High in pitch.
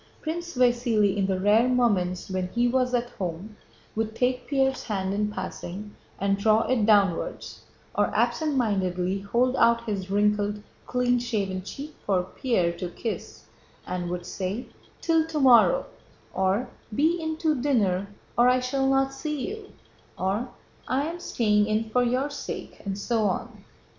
Yes: high, 225 Hz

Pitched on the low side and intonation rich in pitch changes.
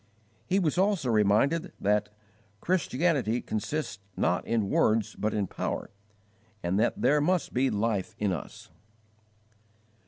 Yes: low, 115 Hz; wide, 6.9 semitones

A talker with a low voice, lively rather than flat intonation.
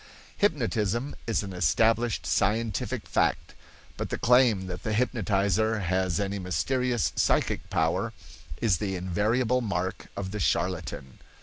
No: low, 105 Hz; average, 3.8 semitones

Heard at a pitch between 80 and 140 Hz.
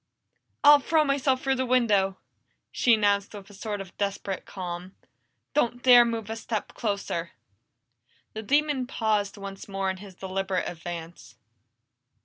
No: high, 205 Hz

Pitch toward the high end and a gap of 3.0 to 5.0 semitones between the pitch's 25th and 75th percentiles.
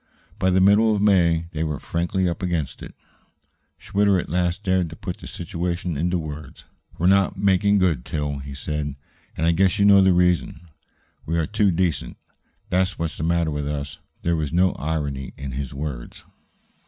No: very low, 85 Hz; average, 3.6 semitones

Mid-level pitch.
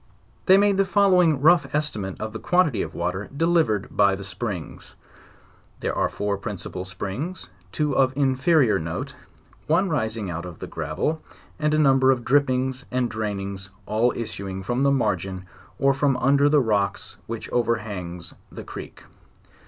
No: low, 120 Hz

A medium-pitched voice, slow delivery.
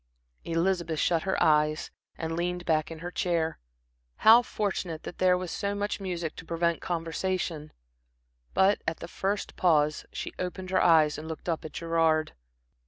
No: medium, 170 Hz; average, 165 wpm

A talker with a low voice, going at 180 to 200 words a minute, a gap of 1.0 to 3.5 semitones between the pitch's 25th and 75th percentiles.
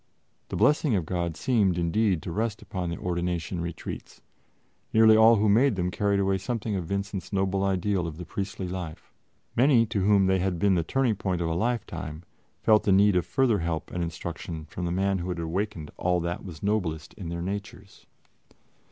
Yes: very low, 95 Hz; average, 195 wpm; average, 3.2 semitones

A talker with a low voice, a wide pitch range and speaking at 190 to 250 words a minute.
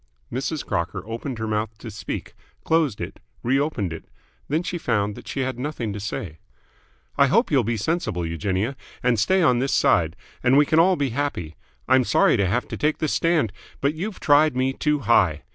Yes: low, 125 Hz; wide, 6.1 semitones; average, 200 wpm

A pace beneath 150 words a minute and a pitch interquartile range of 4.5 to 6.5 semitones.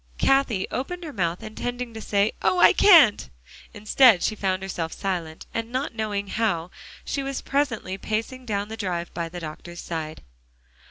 No: average, 165 wpm; wide, 5.6 semitones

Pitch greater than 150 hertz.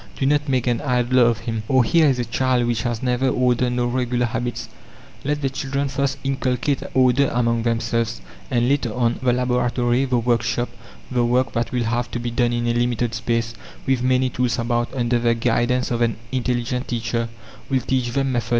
No: low, 120 Hz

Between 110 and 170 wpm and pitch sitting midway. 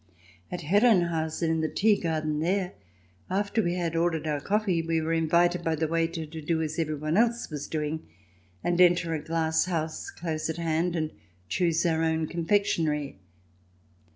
Yes: average, 165 wpm; medium, 165 Hz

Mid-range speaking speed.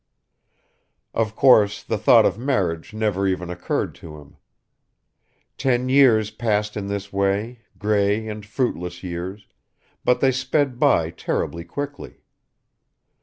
No: slow, 120 wpm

